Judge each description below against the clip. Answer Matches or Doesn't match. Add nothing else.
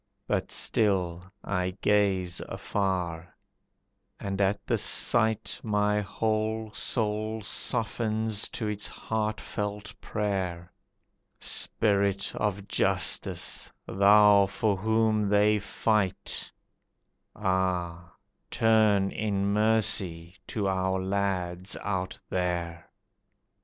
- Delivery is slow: Matches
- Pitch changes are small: Matches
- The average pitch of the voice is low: Matches